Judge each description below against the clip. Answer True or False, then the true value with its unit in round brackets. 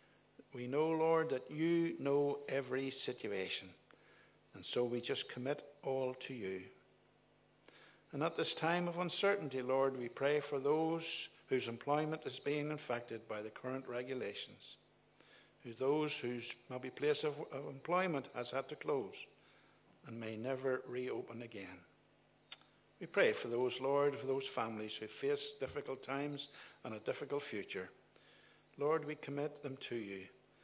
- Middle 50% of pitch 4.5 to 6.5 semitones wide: False (3.3 semitones)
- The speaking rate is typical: True (145 wpm)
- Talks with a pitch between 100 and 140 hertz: True (135 Hz)